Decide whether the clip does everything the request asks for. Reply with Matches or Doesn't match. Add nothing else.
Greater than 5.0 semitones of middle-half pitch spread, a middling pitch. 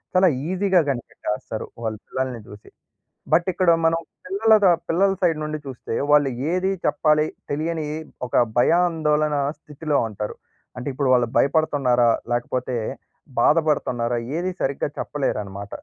Matches